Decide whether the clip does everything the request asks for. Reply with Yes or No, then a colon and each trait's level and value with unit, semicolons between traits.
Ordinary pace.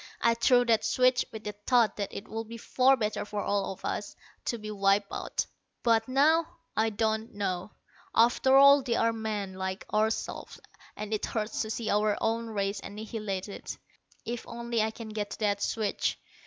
Yes: average, 180 wpm